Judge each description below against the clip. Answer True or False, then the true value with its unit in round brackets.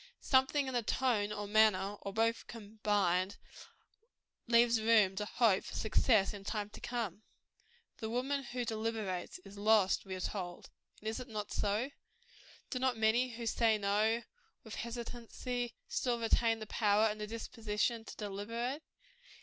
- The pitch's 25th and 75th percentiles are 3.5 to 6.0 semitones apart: False (2.4 semitones)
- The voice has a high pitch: True (220 Hz)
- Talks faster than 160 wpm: False (155 wpm)